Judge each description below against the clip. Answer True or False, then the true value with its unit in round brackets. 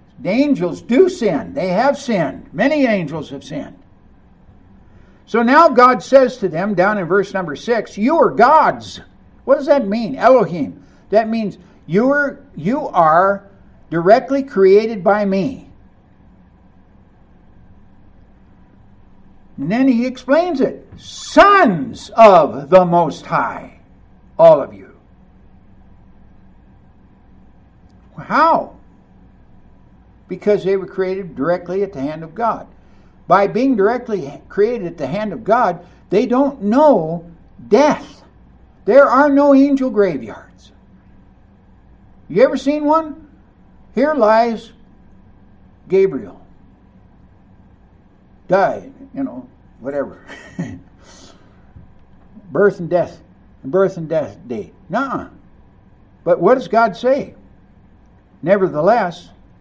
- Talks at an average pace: False (110 wpm)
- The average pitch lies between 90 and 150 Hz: False (185 Hz)